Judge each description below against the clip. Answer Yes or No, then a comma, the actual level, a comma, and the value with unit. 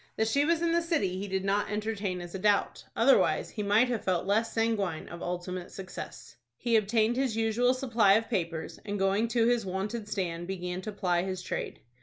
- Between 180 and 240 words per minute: Yes, average, 200 wpm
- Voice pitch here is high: Yes, high, 205 Hz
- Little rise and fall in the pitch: No, average, 3.4 semitones